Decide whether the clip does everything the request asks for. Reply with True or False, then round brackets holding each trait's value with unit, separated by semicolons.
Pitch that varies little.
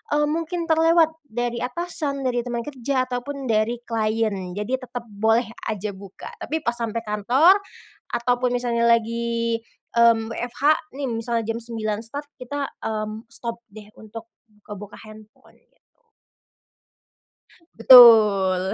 False (3.0 semitones)